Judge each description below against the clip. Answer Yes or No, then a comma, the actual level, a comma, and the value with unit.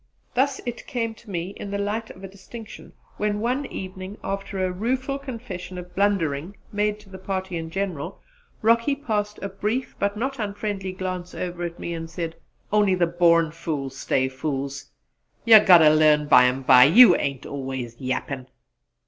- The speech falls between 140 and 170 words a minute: Yes, average, 165 wpm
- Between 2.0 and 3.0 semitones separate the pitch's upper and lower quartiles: No, average, 4.4 semitones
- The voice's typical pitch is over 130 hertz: Yes, high, 190 Hz